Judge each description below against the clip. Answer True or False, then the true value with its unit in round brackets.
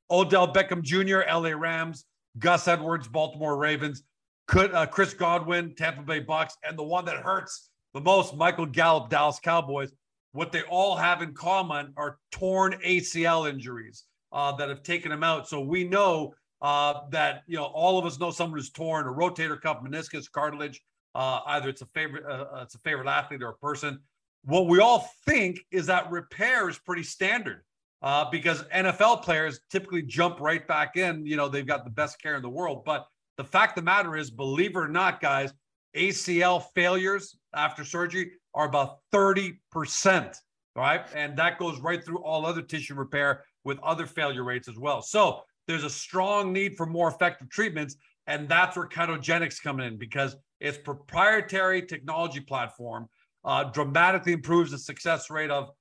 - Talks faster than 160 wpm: True (175 wpm)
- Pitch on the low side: False (160 Hz)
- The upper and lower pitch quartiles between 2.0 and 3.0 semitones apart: False (3.4 semitones)